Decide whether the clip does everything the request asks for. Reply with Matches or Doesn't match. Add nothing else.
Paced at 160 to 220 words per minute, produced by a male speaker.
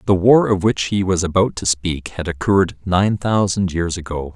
Matches